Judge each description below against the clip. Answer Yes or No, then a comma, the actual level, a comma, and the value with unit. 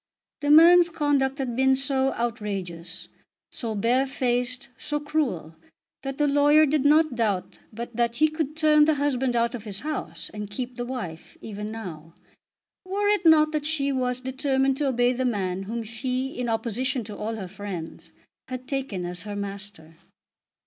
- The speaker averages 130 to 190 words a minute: Yes, average, 170 wpm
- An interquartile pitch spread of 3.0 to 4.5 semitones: No, average, 5.3 semitones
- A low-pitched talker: No, very high, 250 Hz